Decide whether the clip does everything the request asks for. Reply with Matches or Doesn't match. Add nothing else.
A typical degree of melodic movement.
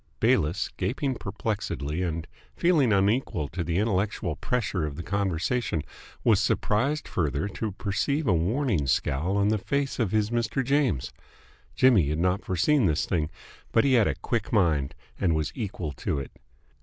Doesn't match